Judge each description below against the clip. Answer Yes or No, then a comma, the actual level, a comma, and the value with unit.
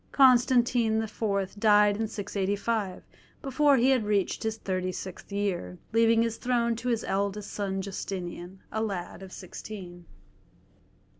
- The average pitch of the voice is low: No, high, 210 Hz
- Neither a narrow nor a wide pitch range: Yes, average, 3.1 semitones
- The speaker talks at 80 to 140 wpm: Yes, slow, 135 wpm